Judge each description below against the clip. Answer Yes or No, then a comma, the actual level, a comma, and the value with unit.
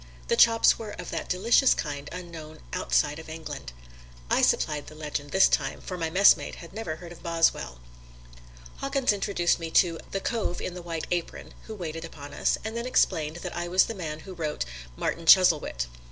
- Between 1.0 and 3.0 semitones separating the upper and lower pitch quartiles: No, average, 3.6 semitones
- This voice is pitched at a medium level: Yes, medium, 170 Hz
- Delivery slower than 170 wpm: No, average, 190 wpm